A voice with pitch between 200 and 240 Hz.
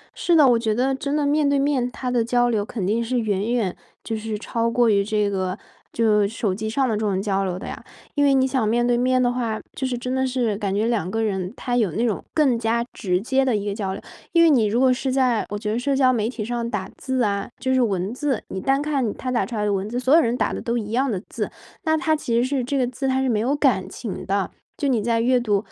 Yes: high, 235 Hz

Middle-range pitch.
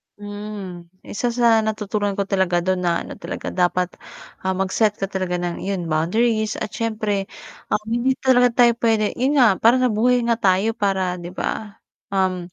No: high, 205 Hz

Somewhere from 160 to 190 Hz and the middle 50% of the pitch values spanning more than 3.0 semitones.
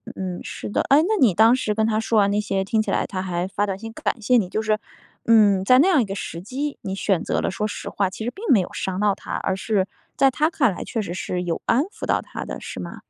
No: high, 210 Hz; average, 3.6 semitones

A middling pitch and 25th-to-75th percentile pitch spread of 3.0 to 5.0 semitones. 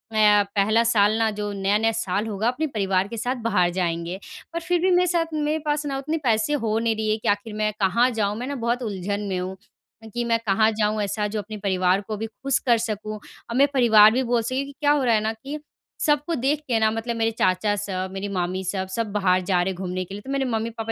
No: high, 220 Hz; average, 3.4 semitones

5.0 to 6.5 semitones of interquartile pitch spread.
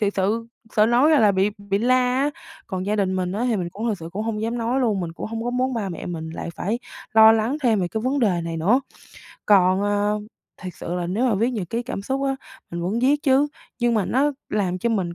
No: average, 4.3 semitones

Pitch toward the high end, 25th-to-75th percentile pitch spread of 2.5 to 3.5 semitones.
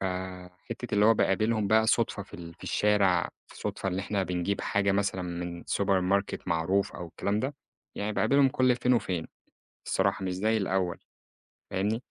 No: low, 100 Hz; average, 2.9 semitones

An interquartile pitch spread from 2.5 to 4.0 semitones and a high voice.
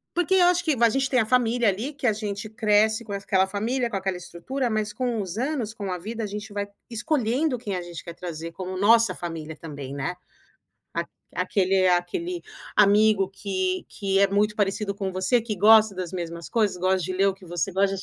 Yes: average, 3.6 semitones; high, 205 Hz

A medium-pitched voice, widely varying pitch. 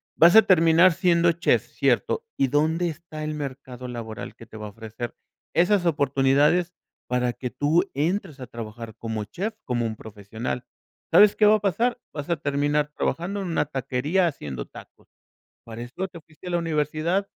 Yes: medium, 150 Hz; wide, 5.9 semitones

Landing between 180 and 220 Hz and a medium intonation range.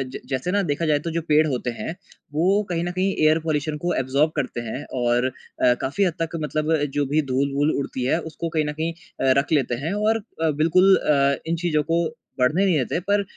No: medium, 155 Hz; average, 3.5 semitones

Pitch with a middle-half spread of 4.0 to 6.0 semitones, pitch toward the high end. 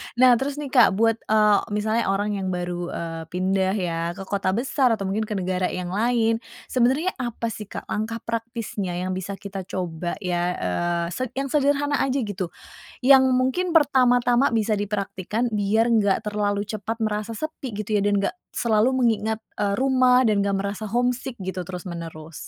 Yes: average, 4.4 semitones; high, 210 Hz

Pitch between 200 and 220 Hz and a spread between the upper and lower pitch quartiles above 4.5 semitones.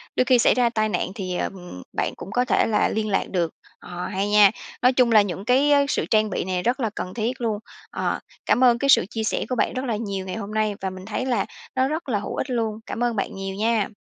No: high, 215 Hz; average, 4.0 semitones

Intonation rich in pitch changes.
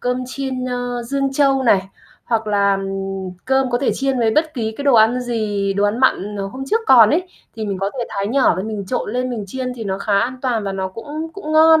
No: average, 4.5 semitones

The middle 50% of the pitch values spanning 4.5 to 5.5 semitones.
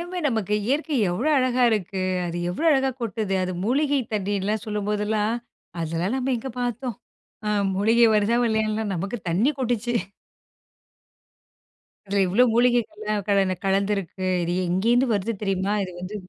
No: average, 3.7 semitones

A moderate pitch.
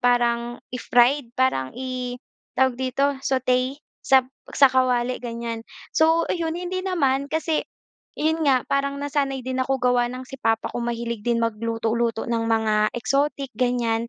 No: very high, 255 Hz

